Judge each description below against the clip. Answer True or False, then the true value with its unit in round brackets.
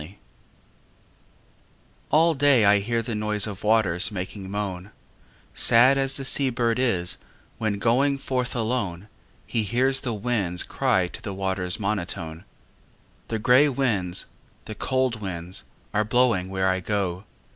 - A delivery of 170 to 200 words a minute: False (140 wpm)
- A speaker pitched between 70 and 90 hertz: False (105 Hz)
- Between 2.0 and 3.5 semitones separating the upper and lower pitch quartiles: False (4.6 semitones)